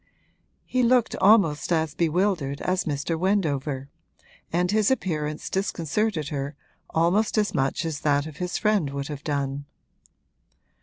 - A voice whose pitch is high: No, medium, 160 Hz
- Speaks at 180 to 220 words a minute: No, slow, 135 wpm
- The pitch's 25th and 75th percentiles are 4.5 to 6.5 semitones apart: Yes, average, 5.3 semitones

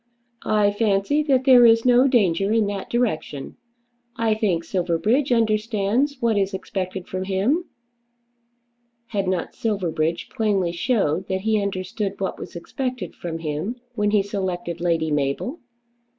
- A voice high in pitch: Yes, high, 200 Hz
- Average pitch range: Yes, average, 4.1 semitones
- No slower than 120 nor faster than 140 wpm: Yes, slow, 135 wpm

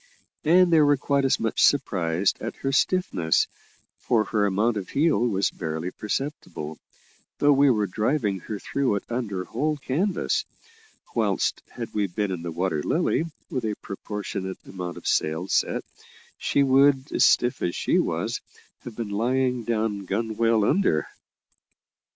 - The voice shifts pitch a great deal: Yes, wide, 6.0 semitones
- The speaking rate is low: No, average, 150 wpm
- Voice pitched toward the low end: Yes, low, 110 Hz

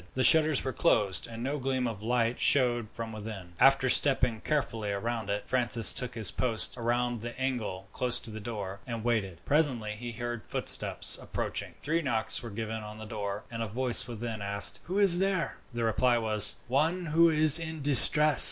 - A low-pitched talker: Yes, low, 120 Hz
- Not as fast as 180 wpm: No, average, 190 wpm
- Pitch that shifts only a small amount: No, average, 3.6 semitones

